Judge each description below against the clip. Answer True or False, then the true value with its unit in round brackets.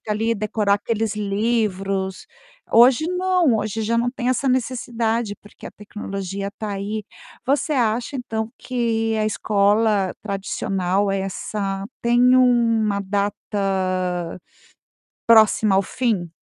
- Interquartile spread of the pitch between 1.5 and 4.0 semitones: True (3.0 semitones)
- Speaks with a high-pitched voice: True (215 Hz)